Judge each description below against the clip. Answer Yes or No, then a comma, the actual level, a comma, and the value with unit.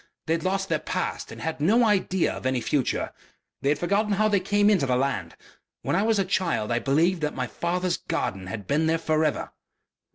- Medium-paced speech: No, fast, 220 wpm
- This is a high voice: No, medium, 165 Hz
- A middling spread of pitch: No, wide, 6.0 semitones